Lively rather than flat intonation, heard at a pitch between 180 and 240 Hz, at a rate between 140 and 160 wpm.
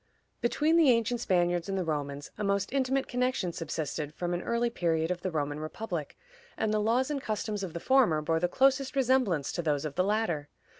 No: wide, 7.0 semitones; high, 190 Hz; fast, 205 wpm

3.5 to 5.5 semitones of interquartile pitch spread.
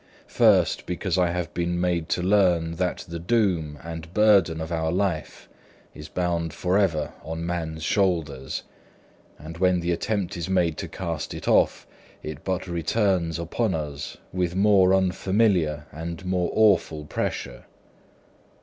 No: narrow, 2.4 semitones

